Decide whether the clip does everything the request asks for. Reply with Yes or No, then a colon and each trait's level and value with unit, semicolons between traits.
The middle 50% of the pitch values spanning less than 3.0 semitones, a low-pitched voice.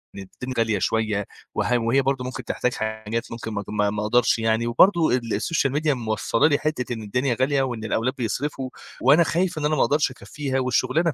No: average, 4.0 semitones; low, 125 Hz